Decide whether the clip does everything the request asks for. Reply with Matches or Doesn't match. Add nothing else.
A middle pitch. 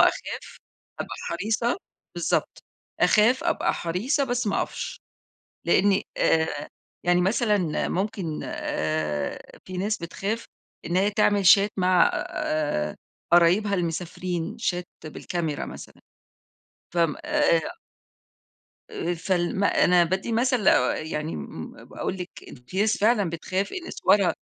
Matches